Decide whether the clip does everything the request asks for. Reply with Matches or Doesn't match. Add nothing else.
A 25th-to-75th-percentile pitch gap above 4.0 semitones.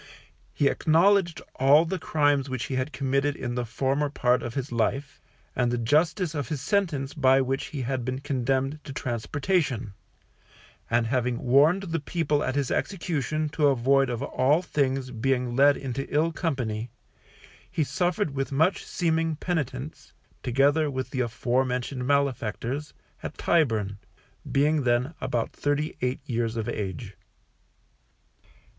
Doesn't match